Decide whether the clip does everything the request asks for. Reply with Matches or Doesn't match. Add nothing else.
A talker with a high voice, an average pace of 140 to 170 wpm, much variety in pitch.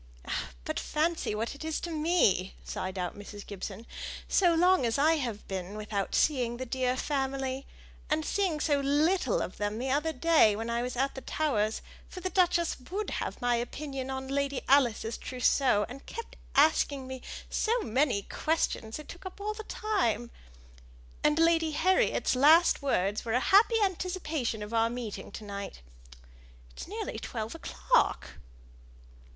Matches